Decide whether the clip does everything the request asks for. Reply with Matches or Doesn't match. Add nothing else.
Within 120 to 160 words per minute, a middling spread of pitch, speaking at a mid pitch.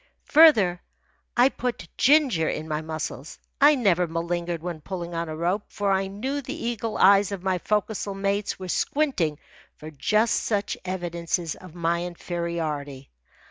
Matches